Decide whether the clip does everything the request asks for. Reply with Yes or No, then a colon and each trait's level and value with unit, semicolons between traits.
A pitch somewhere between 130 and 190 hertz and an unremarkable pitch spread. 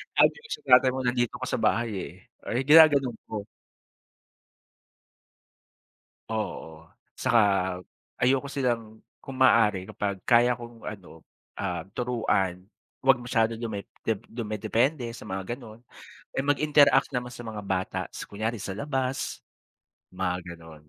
No: low, 115 Hz; average, 4.1 semitones